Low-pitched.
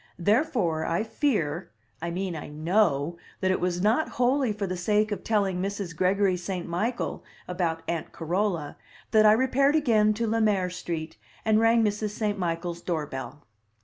No: high, 195 Hz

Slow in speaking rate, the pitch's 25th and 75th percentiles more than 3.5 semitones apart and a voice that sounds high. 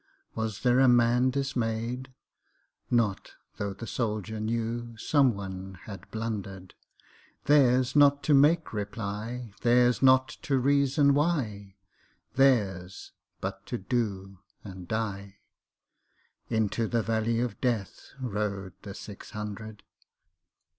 No: slow, 90 wpm; average, 3.9 semitones; low, 115 Hz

